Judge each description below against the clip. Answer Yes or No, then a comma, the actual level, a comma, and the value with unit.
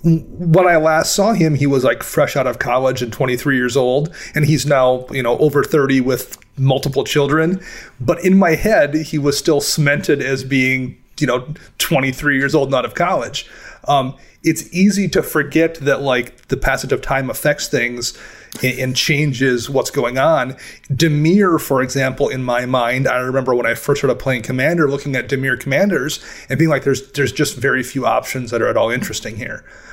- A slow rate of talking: No, average, 195 wpm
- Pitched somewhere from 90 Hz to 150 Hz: Yes, medium, 140 Hz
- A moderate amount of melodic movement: Yes, average, 3.1 semitones